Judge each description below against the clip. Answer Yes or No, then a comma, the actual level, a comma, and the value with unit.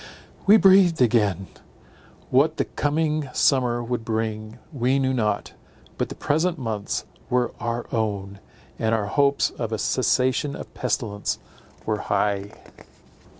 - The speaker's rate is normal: No, slow, 130 wpm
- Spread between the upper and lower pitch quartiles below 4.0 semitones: No, average, 4.6 semitones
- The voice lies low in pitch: Yes, low, 120 Hz